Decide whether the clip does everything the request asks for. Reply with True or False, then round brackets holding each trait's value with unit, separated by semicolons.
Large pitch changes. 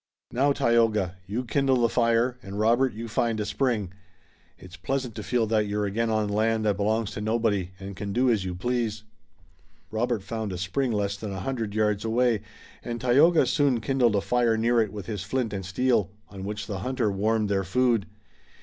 False (3.0 semitones)